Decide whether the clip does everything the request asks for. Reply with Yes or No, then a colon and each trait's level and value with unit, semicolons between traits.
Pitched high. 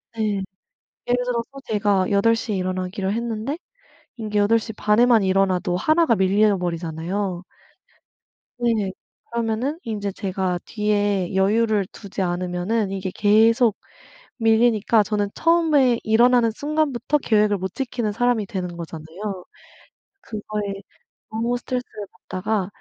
Yes: high, 210 Hz